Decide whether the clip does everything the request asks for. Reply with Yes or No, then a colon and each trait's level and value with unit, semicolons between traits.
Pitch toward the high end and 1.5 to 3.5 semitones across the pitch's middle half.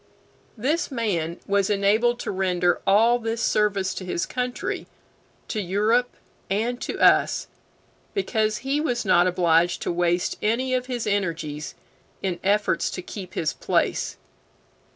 No: high, 205 Hz; average, 5.0 semitones